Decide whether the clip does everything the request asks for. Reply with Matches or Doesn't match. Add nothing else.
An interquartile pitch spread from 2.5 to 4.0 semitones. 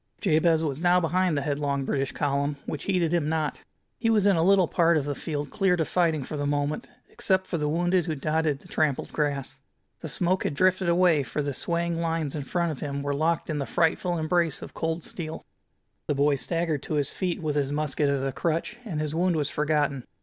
Matches